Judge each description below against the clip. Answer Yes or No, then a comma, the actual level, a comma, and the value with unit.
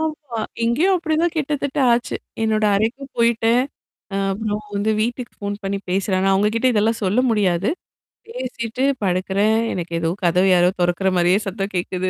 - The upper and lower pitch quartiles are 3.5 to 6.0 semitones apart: Yes, average, 4.1 semitones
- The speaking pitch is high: Yes, high, 215 Hz